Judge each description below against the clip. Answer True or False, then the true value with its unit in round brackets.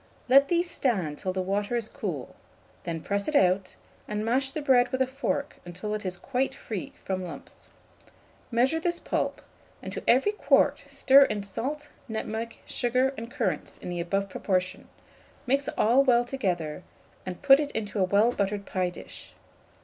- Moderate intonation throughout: False (5.9 semitones)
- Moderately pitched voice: False (225 Hz)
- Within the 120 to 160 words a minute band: False (170 wpm)